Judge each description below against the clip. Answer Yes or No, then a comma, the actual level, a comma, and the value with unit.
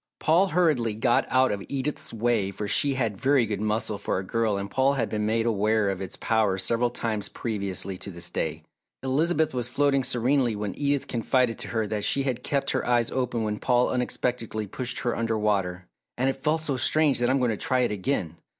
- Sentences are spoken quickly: Yes, fast, 215 wpm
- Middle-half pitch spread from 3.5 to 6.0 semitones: Yes, average, 3.9 semitones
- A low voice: Yes, low, 120 Hz